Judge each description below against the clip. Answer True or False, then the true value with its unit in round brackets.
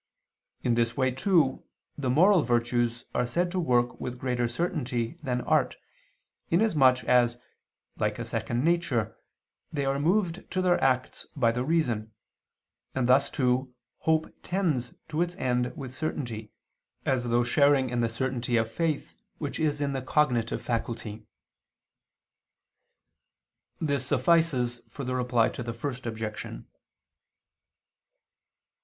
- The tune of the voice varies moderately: True (4.2 semitones)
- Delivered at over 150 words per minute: False (135 wpm)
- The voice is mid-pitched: False (130 Hz)